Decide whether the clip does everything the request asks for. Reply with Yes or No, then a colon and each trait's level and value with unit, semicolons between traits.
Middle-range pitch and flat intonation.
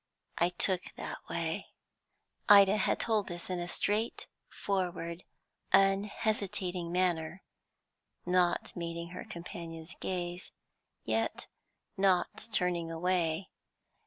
Yes: medium, 180 Hz; narrow, 2.3 semitones